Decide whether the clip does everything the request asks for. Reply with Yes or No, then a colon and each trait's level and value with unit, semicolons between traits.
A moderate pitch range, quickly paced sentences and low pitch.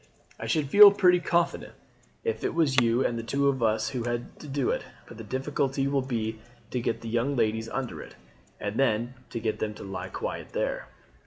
Yes: average, 3.7 semitones; fast, 210 wpm; low, 120 Hz